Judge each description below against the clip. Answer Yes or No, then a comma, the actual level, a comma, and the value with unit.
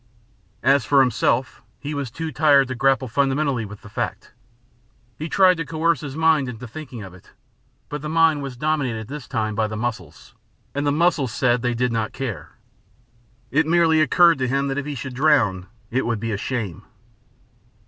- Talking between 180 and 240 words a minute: Yes, average, 190 wpm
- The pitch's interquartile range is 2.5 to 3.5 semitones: No, average, 4.4 semitones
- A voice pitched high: No, low, 135 Hz